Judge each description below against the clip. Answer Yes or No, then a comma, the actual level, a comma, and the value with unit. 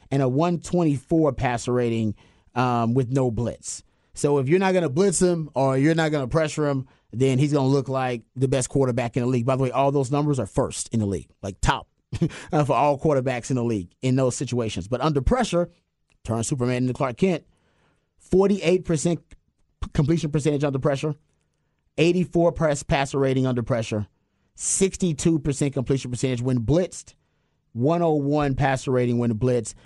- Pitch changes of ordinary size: Yes, average, 4.0 semitones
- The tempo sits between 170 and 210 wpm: Yes, average, 180 wpm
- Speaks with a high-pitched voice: No, low, 135 Hz